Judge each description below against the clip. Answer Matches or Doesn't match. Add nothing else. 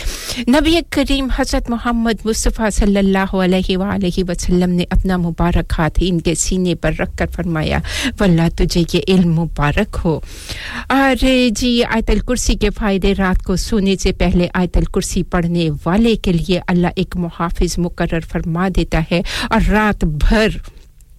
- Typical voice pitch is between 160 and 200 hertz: Matches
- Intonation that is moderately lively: Matches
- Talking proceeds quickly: Doesn't match